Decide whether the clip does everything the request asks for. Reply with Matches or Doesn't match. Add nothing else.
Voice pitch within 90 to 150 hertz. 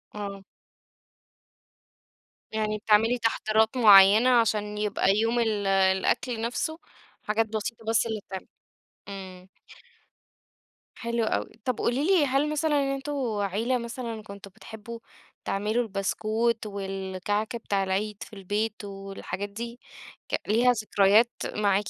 Doesn't match